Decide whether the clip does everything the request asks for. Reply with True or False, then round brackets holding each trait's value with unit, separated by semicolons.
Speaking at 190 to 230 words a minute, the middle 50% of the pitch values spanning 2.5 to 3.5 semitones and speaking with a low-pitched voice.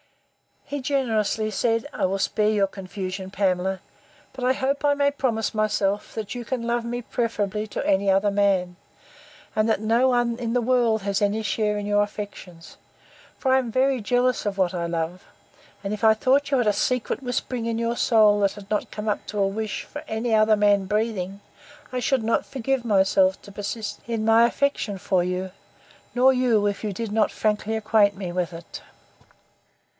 False (195 wpm; 3.2 semitones; 215 Hz)